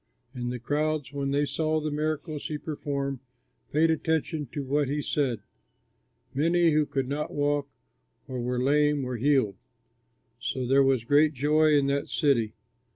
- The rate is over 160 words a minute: No, average, 155 wpm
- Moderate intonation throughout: No, narrow, 2.2 semitones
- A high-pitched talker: No, medium, 145 Hz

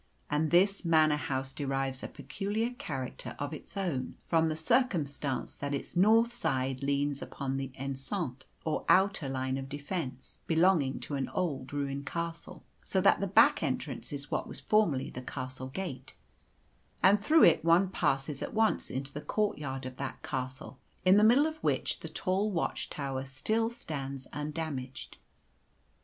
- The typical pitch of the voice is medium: Yes, medium, 145 Hz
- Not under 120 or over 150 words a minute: No, average, 160 wpm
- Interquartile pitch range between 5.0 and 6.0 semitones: Yes, wide, 5.6 semitones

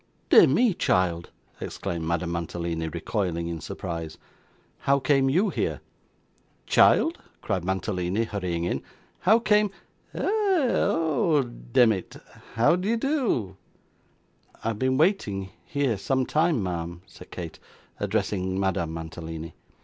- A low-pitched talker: Yes, low, 100 Hz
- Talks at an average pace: No, slow, 120 wpm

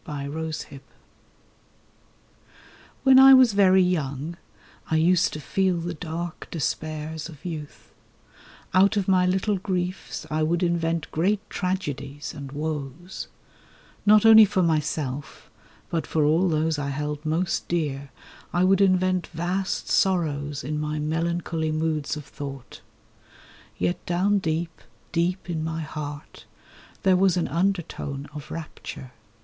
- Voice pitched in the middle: Yes, medium, 165 Hz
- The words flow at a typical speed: No, slow, 130 wpm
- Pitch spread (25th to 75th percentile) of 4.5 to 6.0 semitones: No, average, 3.5 semitones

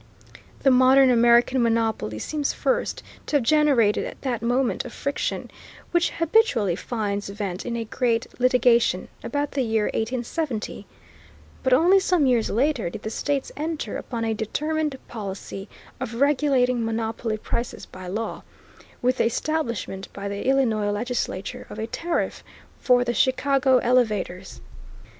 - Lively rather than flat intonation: No, average, 3.8 semitones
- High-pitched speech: Yes, high, 240 Hz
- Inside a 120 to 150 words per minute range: Yes, average, 140 wpm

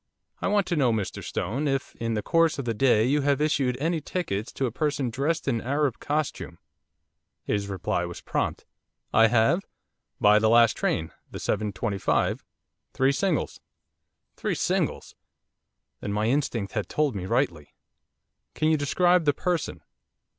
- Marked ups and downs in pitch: Yes, wide, 5.7 semitones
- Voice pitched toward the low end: Yes, low, 130 Hz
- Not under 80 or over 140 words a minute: No, average, 155 wpm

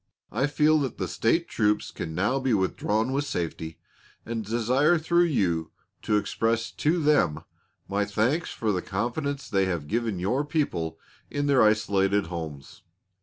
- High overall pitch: No, low, 110 Hz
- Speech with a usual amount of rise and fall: No, wide, 6.8 semitones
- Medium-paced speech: Yes, average, 155 wpm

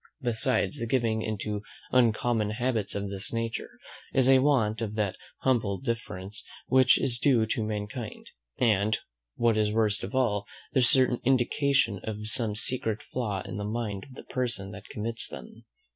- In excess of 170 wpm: No, average, 160 wpm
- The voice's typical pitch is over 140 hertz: No, low, 110 Hz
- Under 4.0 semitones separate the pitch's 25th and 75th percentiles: Yes, average, 3.0 semitones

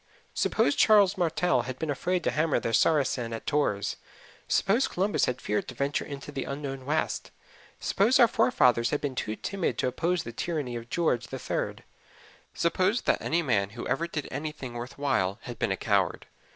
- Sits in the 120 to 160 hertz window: Yes, medium, 140 Hz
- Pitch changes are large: Yes, wide, 5.9 semitones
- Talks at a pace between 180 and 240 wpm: Yes, average, 190 wpm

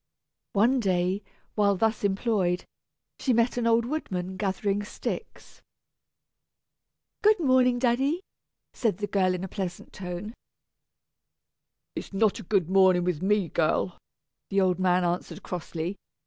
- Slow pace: Yes, slow, 130 wpm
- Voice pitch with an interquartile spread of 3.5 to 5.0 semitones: Yes, average, 4.1 semitones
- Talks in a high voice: Yes, high, 195 Hz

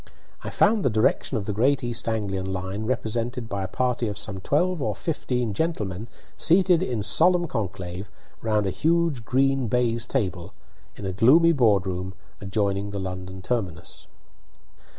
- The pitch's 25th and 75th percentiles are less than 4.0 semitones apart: No, average, 5.3 semitones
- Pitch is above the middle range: No, low, 110 Hz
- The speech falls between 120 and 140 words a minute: No, average, 155 wpm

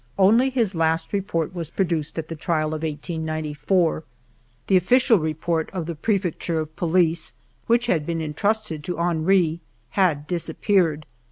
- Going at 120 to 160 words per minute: Yes, average, 150 wpm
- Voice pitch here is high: No, medium, 165 Hz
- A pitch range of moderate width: Yes, average, 3.1 semitones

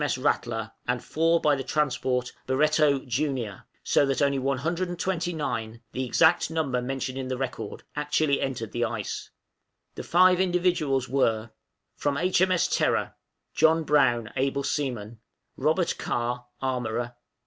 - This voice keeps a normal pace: Yes, average, 150 wpm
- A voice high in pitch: No, low, 135 Hz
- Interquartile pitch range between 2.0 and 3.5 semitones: No, average, 4.3 semitones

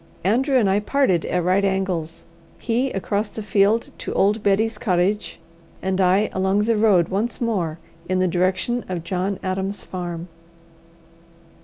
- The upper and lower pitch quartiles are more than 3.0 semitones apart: No, narrow, 2.5 semitones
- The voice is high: Yes, high, 195 Hz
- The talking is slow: No, average, 150 wpm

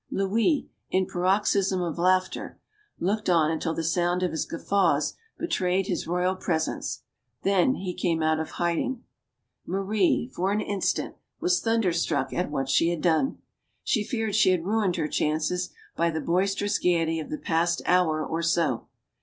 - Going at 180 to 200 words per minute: No, average, 160 wpm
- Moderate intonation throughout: Yes, average, 3.0 semitones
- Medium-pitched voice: Yes, medium, 180 Hz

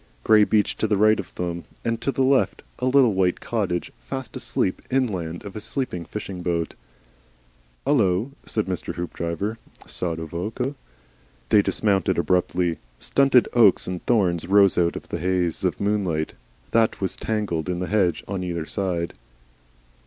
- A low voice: Yes, very low, 95 Hz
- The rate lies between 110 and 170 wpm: Yes, average, 160 wpm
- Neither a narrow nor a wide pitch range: Yes, average, 4.0 semitones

